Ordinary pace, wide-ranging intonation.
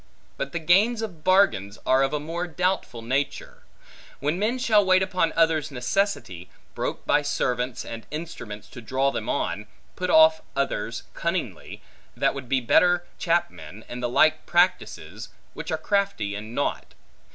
Yes: average, 155 wpm; wide, 6.6 semitones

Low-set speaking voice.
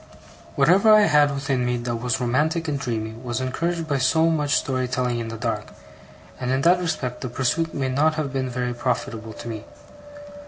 Yes: low, 130 Hz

